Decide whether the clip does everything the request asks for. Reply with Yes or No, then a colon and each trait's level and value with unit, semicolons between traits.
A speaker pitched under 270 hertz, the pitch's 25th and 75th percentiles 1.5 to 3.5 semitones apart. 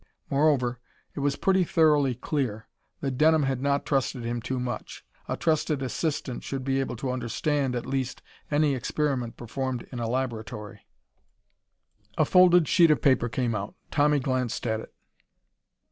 Yes: low, 135 Hz; average, 3.2 semitones